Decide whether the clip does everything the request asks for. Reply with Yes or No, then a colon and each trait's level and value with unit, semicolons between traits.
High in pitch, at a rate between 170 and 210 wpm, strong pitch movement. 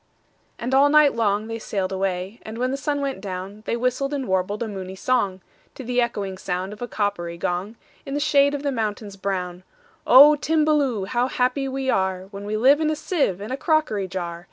Yes: high, 225 Hz; average, 185 wpm; wide, 6.2 semitones